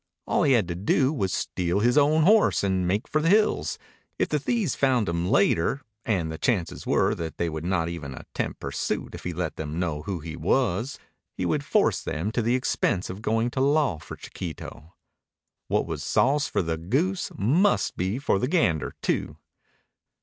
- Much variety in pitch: Yes, wide, 8.3 semitones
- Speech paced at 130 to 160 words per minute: No, average, 195 wpm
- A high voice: No, low, 100 Hz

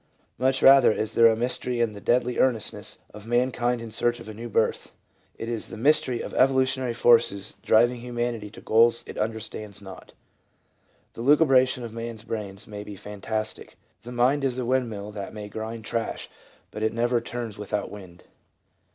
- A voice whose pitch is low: Yes, low, 115 Hz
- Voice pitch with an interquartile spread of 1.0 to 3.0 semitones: Yes, narrow, 2.4 semitones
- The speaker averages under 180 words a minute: No, average, 185 wpm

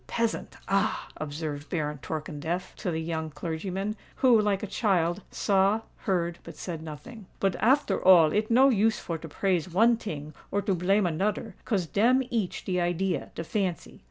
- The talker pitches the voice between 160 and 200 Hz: Yes, medium, 185 Hz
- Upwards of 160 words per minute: No, average, 155 wpm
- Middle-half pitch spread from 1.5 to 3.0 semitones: No, average, 4.5 semitones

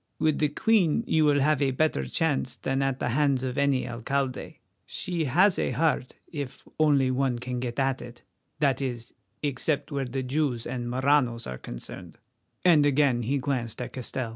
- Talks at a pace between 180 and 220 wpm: No, average, 170 wpm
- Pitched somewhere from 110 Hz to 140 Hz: Yes, low, 135 Hz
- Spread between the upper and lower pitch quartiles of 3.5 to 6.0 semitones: No, average, 2.9 semitones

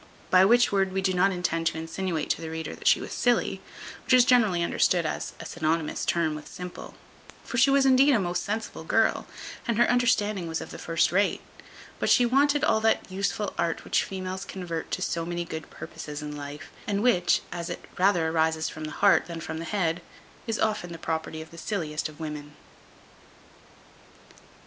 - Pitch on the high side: No, medium, 175 Hz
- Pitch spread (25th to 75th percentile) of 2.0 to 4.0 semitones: No, average, 4.5 semitones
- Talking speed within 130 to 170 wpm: No, average, 195 wpm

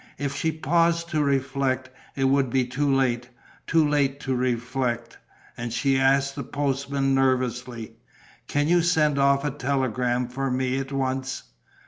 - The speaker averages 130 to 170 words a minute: Yes, average, 150 wpm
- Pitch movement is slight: Yes, narrow, 1.8 semitones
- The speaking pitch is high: No, low, 135 Hz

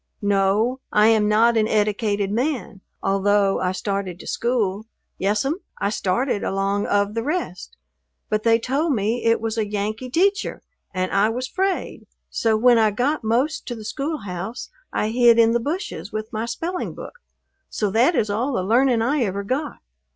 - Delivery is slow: No, average, 175 wpm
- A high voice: Yes, high, 220 Hz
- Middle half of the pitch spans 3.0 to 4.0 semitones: Yes, average, 3.7 semitones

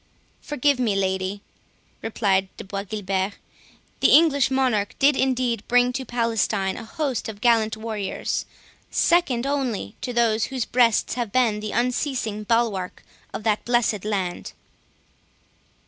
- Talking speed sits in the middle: No, slow, 130 wpm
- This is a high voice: Yes, high, 230 Hz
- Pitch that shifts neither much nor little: Yes, average, 3.6 semitones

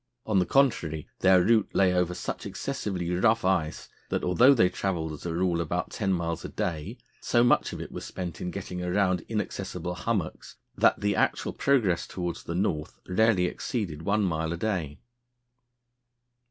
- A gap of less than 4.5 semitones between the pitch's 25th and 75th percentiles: Yes, average, 3.3 semitones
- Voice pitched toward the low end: Yes, very low, 90 Hz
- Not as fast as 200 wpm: Yes, average, 170 wpm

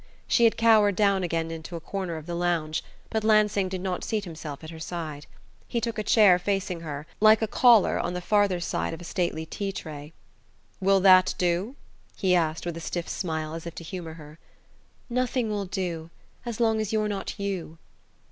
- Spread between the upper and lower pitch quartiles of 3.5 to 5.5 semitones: Yes, average, 4.1 semitones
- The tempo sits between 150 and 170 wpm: No, average, 200 wpm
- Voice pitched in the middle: Yes, medium, 180 Hz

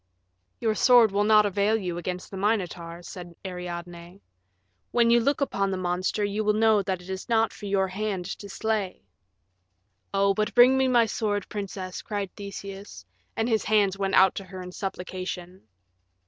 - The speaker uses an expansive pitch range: No, average, 2.7 semitones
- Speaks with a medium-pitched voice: No, high, 200 Hz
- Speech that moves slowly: No, average, 175 wpm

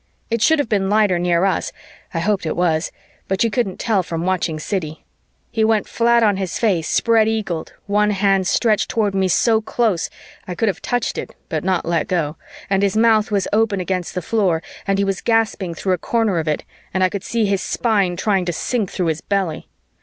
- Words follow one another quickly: Yes, fast, 215 wpm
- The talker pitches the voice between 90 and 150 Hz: No, high, 195 Hz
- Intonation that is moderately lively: Yes, average, 3.5 semitones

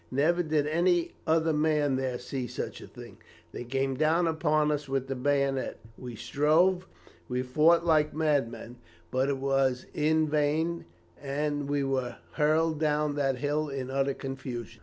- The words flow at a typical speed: Yes, average, 160 wpm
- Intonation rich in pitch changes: No, narrow, 2.6 semitones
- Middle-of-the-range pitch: Yes, medium, 145 Hz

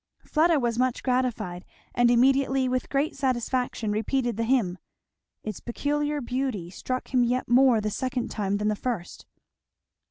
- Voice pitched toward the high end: Yes, very high, 250 Hz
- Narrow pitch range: No, average, 3.3 semitones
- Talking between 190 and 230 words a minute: No, average, 150 wpm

